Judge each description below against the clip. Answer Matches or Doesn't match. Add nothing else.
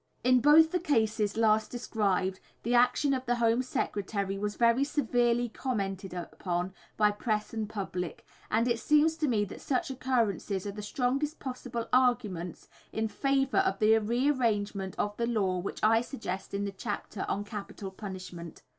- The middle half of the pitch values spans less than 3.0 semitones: Doesn't match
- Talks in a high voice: Matches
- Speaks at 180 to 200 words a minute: Doesn't match